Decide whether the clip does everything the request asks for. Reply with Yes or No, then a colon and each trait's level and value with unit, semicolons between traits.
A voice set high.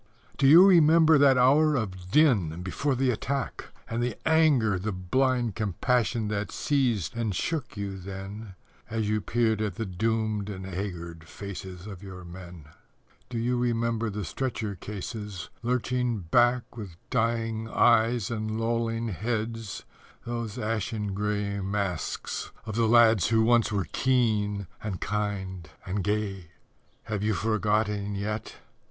No: low, 110 Hz